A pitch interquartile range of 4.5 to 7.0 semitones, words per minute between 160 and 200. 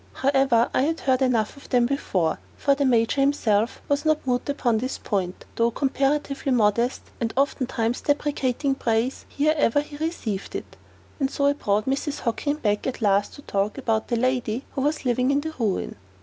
No: average, 3.8 semitones; average, 185 wpm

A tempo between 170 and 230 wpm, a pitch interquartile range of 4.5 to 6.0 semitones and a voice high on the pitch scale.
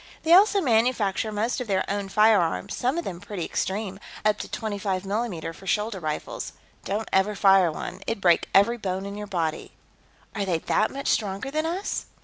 No: average, 185 wpm; average, 2.9 semitones; high, 205 Hz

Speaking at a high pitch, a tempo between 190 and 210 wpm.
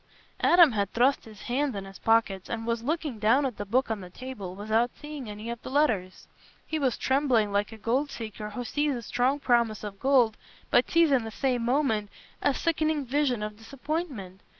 Yes: high, 240 Hz; average, 200 wpm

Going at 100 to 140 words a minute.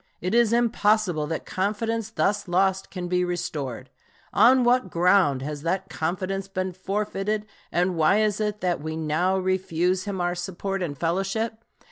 No: average, 155 wpm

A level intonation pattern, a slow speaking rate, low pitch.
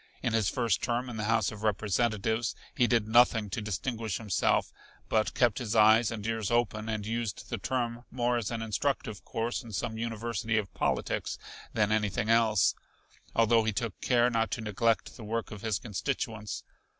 No: narrow, 1.7 semitones; average, 180 wpm; low, 115 Hz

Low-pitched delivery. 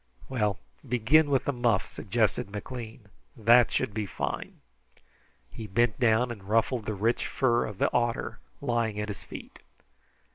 Yes: low, 115 Hz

